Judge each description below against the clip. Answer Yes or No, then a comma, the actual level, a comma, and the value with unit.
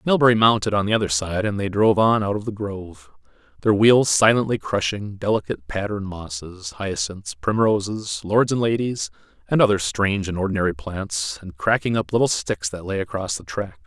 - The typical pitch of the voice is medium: No, low, 100 Hz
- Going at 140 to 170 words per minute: No, average, 180 wpm